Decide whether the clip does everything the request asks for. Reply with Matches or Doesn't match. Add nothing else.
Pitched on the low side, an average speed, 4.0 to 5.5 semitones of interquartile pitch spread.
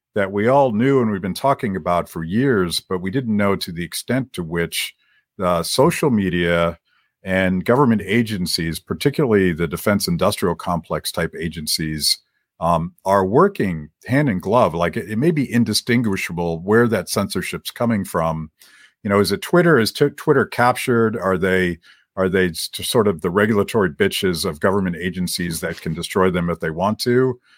Matches